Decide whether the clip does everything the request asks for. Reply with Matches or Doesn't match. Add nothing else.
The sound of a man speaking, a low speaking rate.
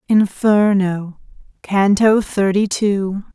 Doesn't match